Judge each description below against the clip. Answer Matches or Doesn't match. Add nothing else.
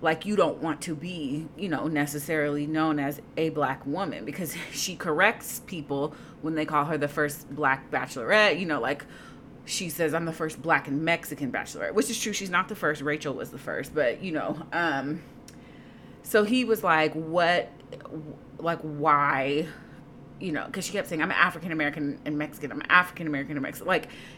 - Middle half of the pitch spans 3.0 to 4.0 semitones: Doesn't match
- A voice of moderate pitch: Matches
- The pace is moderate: Matches